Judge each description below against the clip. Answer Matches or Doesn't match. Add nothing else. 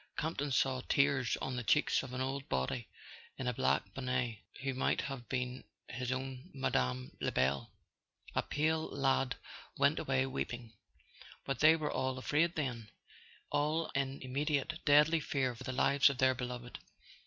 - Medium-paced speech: Matches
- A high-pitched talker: Doesn't match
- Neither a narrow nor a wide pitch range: Doesn't match